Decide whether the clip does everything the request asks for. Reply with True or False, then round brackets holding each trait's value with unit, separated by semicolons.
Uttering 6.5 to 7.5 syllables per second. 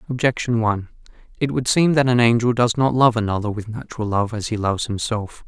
False (6.1 syllables/s)